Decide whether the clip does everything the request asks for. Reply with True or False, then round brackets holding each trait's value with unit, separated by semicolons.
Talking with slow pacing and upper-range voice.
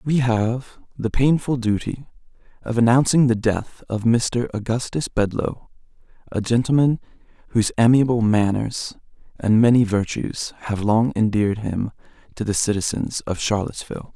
False (125 wpm; 115 Hz)